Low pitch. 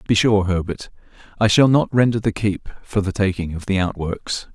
Yes: low, 100 Hz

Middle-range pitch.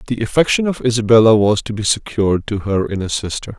No: low, 110 Hz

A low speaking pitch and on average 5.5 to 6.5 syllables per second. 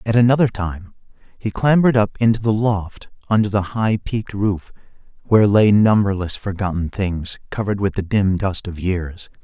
No: low, 100 Hz; 5.1 syllables/s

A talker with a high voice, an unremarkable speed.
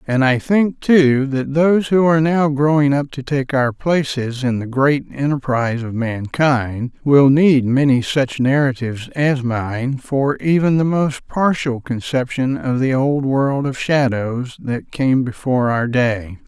No: low, 135 Hz; average, 165 wpm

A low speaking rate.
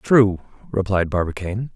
Yes: slow, 105 wpm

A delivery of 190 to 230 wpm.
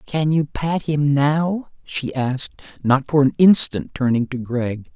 No: average, 170 wpm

